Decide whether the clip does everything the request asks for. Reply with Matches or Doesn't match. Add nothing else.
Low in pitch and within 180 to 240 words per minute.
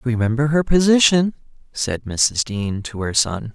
Doesn't match